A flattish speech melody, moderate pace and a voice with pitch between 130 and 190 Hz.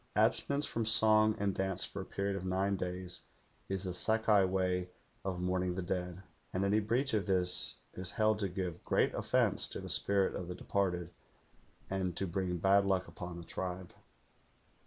No: narrow, 1.8 semitones; average, 180 wpm; very low, 95 Hz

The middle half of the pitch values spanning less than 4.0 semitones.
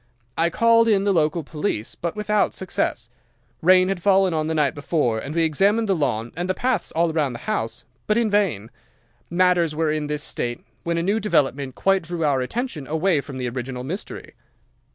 No: average, 5.1 semitones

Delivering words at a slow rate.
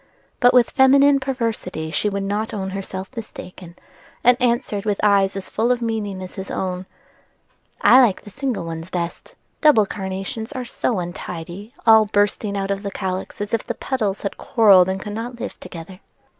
No: average, 180 wpm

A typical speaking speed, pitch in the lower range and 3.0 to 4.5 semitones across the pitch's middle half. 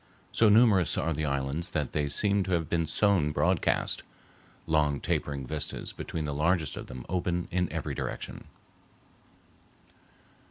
Yes: average, 145 wpm; very low, 80 Hz; average, 3.6 semitones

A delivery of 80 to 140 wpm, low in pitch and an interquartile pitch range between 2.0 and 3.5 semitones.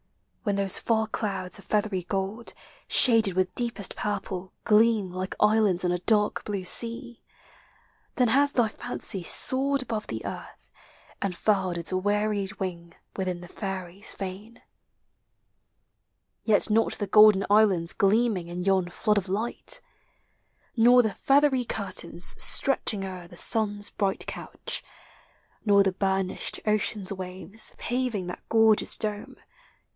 No: slow, 135 wpm; high, 205 Hz; average, 3.0 semitones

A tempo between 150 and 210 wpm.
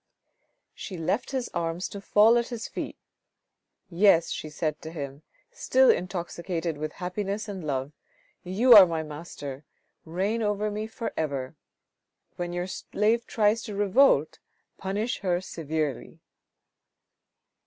No: average, 140 wpm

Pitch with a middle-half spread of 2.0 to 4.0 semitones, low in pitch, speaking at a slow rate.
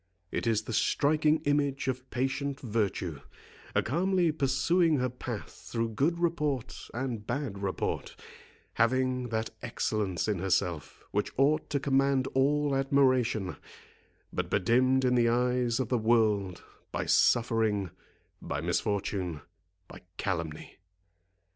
No: average, 4.7 semitones; low, 125 Hz; slow, 120 wpm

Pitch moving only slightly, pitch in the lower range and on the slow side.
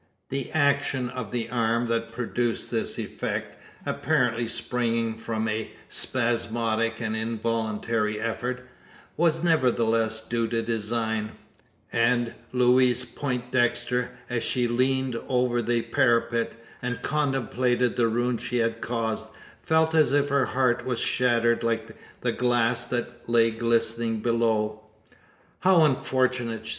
Yes: narrow, 1.6 semitones; low, 120 Hz; slow, 120 wpm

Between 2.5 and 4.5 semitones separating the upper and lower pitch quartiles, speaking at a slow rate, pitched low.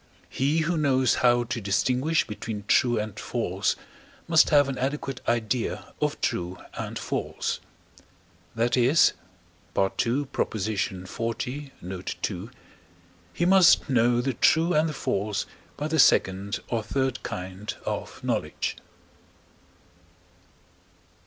No: average, 5.2 semitones; slow, 115 wpm; low, 120 Hz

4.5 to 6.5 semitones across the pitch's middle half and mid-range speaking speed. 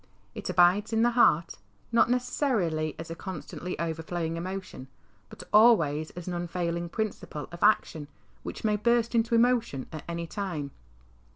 Yes: average, 5.3 semitones; average, 150 wpm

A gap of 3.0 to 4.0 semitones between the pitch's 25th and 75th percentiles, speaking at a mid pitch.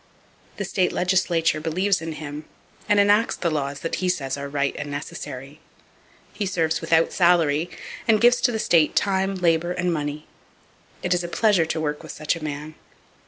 Yes: average, 3.5 semitones; medium, 165 Hz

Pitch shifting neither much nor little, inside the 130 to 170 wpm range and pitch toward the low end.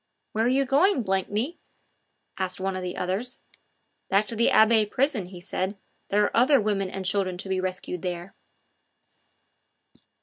No: average, 3.8 semitones; average, 160 wpm; high, 200 Hz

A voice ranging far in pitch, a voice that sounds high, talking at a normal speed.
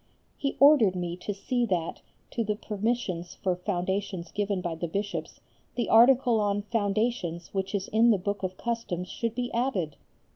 No: average, 4.2 semitones; high, 205 Hz; average, 170 wpm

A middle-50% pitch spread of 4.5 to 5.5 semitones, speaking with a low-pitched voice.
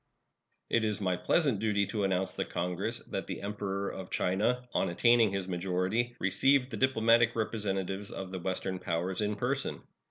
No: average, 3.5 semitones; low, 100 Hz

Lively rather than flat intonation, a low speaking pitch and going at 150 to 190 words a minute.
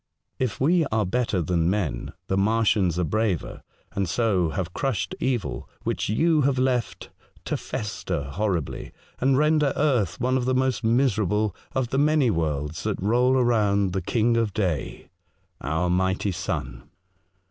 Yes: wide, 5.8 semitones; low, 105 Hz; average, 155 wpm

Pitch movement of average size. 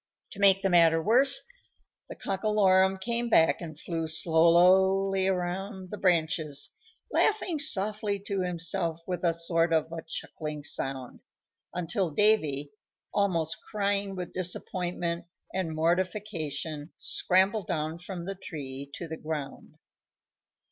Yes: average, 3.2 semitones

